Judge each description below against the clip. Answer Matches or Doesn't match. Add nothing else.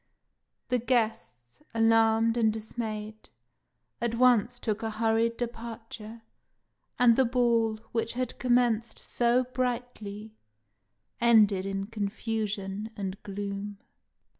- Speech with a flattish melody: Matches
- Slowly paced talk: Matches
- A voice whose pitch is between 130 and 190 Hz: Doesn't match